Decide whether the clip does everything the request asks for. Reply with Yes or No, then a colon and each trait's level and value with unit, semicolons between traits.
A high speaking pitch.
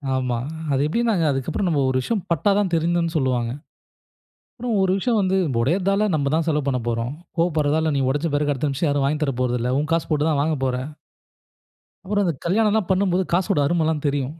No: medium, 155 Hz